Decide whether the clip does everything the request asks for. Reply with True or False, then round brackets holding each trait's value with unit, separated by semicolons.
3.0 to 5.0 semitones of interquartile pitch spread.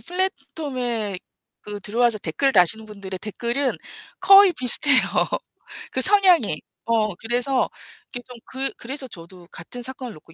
True (4.7 semitones)